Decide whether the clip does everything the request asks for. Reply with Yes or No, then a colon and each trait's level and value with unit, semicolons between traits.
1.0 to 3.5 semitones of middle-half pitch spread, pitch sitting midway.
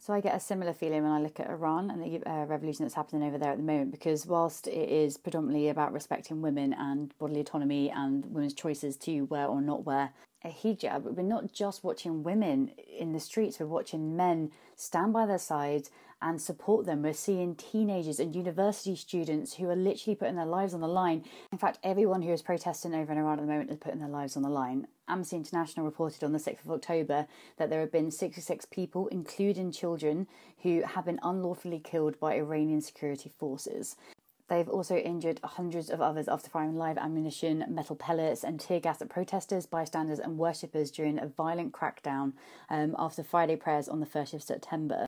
Yes: average, 2.8 semitones; medium, 160 Hz